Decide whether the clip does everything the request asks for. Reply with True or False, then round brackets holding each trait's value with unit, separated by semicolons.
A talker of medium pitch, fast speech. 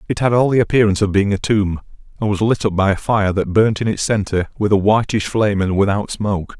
False (105 Hz; 255 wpm)